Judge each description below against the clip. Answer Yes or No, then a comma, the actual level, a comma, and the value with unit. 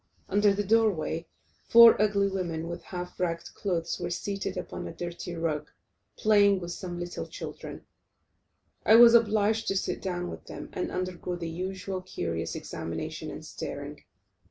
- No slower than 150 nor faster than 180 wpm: Yes, average, 155 wpm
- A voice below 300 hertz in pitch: Yes, medium, 185 Hz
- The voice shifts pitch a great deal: No, average, 3.0 semitones